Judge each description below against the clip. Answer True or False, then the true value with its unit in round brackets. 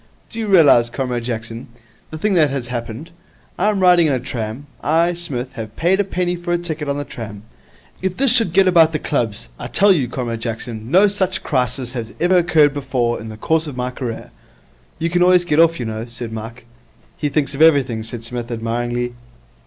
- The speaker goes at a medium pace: False (210 wpm)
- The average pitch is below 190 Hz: True (140 Hz)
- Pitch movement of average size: False (6.5 semitones)